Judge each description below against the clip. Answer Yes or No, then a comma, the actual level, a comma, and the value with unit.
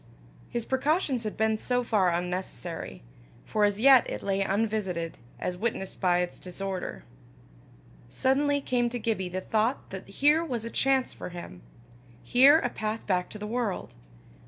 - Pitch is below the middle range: No, high, 215 Hz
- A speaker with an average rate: Yes, average, 155 wpm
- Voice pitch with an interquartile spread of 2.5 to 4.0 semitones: No, average, 5.1 semitones